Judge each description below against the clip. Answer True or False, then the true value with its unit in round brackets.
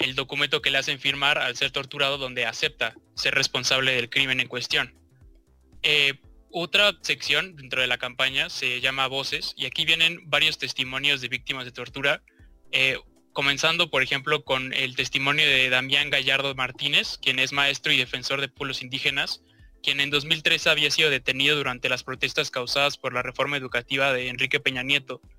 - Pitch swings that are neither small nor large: False (2.2 semitones)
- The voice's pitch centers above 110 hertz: True (135 Hz)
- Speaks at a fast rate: False (175 wpm)